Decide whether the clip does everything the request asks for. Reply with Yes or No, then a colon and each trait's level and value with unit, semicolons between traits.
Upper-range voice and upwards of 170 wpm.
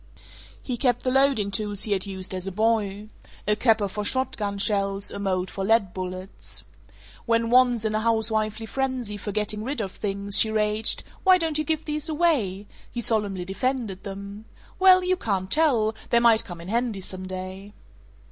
Yes: high, 215 Hz; average, 185 wpm